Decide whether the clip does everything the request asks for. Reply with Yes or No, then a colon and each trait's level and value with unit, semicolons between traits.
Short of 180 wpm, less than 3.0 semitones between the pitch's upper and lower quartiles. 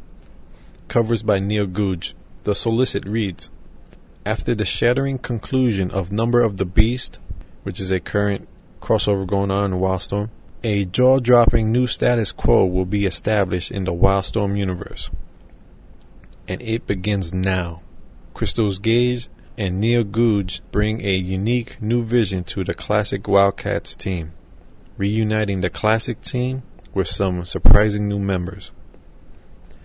No: slow, 135 wpm; average, 3.5 semitones